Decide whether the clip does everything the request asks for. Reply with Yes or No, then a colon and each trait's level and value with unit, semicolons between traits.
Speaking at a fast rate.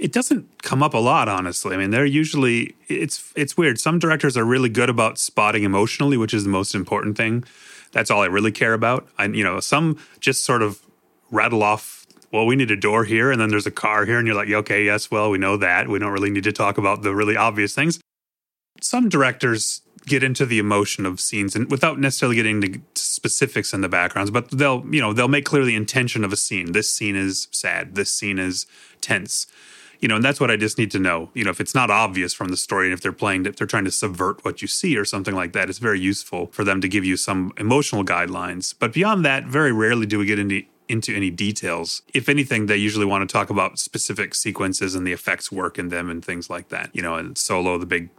Yes: fast, 245 wpm